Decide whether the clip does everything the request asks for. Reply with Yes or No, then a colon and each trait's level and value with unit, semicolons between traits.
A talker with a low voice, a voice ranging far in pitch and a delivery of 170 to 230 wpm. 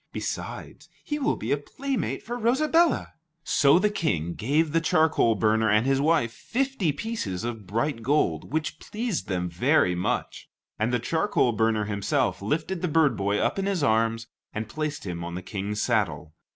Yes: low, 130 Hz; wide, 7.9 semitones; average, 175 wpm